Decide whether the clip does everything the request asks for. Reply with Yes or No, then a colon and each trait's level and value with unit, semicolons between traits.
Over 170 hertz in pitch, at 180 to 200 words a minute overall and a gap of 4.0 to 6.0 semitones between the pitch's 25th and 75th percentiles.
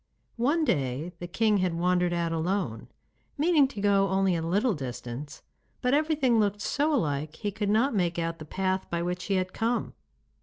Yes: high, 190 Hz; average, 185 wpm; average, 5.0 semitones